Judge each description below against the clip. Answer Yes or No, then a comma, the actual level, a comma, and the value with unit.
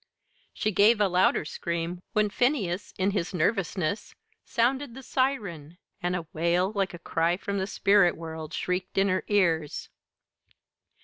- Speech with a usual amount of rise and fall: Yes, average, 3.3 semitones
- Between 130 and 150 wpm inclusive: Yes, average, 145 wpm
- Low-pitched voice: No, medium, 185 Hz